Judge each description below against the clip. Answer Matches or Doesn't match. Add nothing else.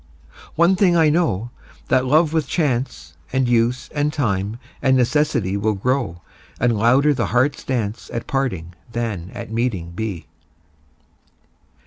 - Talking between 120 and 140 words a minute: Matches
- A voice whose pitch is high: Doesn't match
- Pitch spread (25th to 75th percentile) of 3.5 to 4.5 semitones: Doesn't match